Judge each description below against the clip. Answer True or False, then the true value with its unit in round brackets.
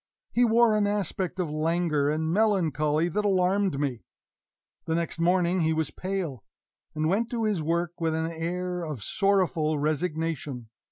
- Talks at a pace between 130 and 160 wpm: True (155 wpm)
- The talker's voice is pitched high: False (170 Hz)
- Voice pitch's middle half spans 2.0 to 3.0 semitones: False (3.6 semitones)